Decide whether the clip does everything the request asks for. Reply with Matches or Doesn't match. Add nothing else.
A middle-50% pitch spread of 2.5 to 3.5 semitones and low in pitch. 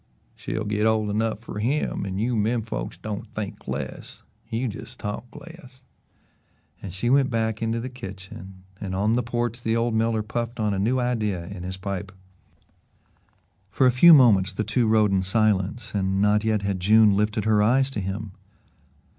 Matches